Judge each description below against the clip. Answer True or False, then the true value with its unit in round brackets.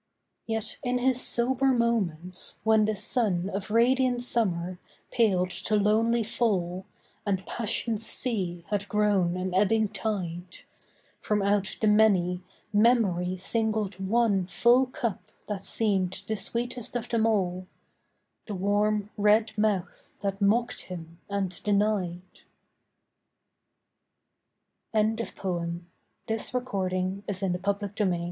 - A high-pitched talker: True (205 Hz)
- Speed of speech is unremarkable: False (125 wpm)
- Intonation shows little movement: False (3.3 semitones)